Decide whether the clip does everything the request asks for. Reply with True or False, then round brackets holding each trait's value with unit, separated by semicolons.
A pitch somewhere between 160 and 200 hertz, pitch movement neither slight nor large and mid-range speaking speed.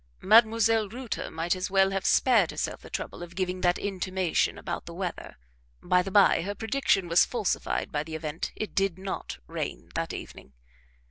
True (190 Hz; 3.2 semitones; 180 wpm)